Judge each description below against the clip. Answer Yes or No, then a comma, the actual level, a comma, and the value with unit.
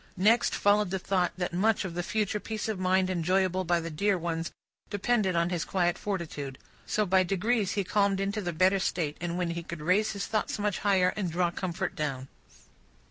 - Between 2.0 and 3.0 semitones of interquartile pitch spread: Yes, average, 2.7 semitones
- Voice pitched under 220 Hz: Yes, medium, 185 Hz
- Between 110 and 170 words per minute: No, average, 195 wpm